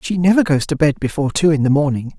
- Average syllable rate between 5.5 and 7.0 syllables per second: Yes, 6.7 syllables/s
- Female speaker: No, male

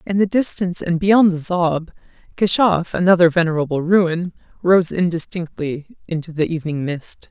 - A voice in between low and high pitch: Yes, medium, 175 Hz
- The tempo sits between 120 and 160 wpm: Yes, average, 140 wpm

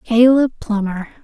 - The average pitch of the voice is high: Yes, high, 230 Hz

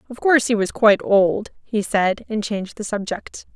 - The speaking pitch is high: Yes, high, 210 Hz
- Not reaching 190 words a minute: No, fast, 205 wpm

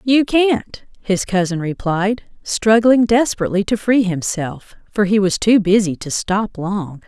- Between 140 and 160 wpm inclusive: Yes, average, 155 wpm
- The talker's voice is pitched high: Yes, high, 205 Hz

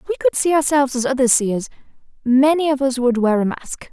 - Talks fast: Yes, fast, 245 wpm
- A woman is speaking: Yes, female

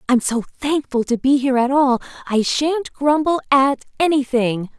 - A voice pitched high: Yes, very high, 270 Hz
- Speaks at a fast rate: No, average, 165 wpm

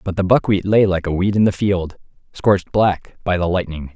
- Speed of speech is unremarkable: No, fast, 230 wpm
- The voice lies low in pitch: Yes, very low, 95 Hz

